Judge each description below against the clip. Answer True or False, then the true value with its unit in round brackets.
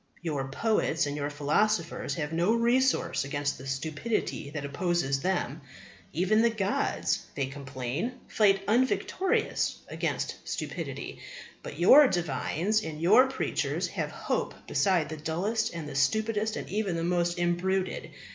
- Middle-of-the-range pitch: True (175 Hz)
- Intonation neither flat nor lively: False (6.6 semitones)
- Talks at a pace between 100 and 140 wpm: True (135 wpm)